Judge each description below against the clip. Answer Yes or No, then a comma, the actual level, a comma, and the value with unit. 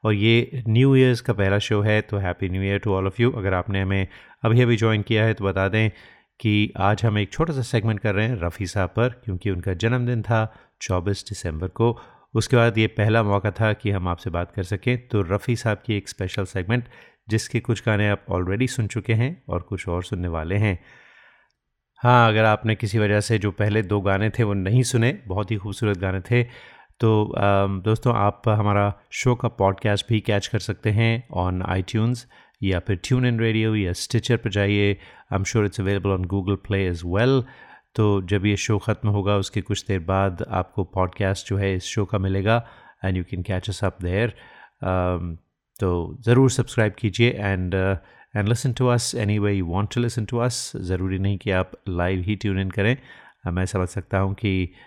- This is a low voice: Yes, low, 105 Hz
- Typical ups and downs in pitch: Yes, average, 3.0 semitones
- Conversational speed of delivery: No, fast, 205 wpm